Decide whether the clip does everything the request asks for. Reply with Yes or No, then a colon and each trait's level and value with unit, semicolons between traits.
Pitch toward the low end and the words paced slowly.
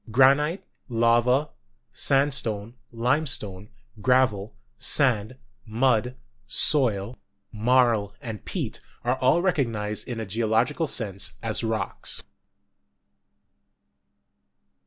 Yes: low, 120 Hz; slow, 85 wpm